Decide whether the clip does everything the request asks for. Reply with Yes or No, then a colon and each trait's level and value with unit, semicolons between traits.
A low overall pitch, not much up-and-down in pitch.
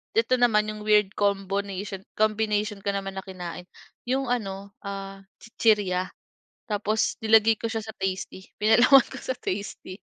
No: high, 205 Hz; narrow, 2.1 semitones